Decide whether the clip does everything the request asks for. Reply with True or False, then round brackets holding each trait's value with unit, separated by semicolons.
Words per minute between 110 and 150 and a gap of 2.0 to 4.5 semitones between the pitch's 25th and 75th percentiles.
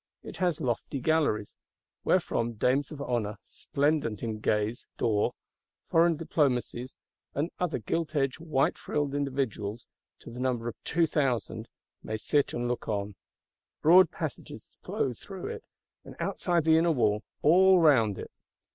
False (140 wpm; 5.3 semitones)